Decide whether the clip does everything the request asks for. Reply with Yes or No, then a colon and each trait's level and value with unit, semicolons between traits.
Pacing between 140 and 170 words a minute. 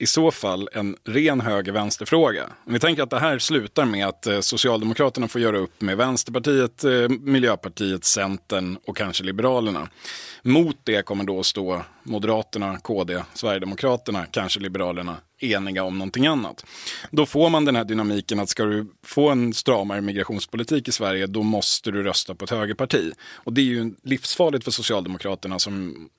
Yes: average, 165 wpm